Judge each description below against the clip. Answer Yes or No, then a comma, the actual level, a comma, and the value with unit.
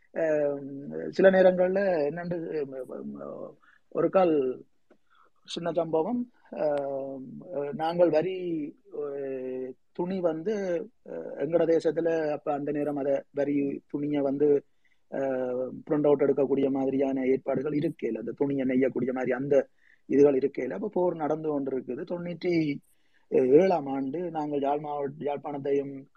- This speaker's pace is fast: No, average, 100 wpm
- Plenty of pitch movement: No, average, 3.8 semitones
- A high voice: No, medium, 145 Hz